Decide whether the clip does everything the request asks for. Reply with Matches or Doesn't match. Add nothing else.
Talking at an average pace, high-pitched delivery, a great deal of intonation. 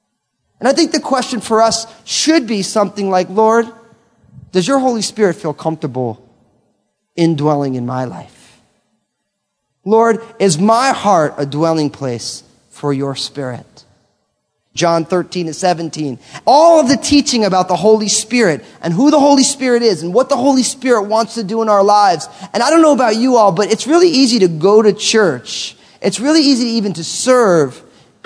Matches